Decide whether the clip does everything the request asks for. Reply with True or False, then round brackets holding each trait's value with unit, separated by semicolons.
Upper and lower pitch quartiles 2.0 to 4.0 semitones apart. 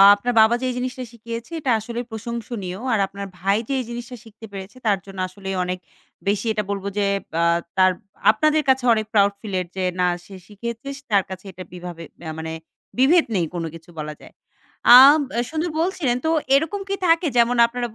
False (4.5 semitones)